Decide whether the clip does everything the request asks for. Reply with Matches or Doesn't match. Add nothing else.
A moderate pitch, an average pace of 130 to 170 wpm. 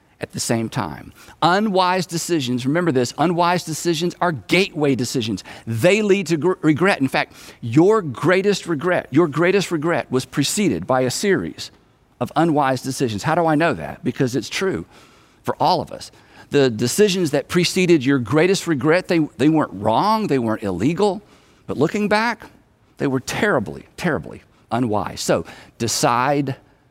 Matches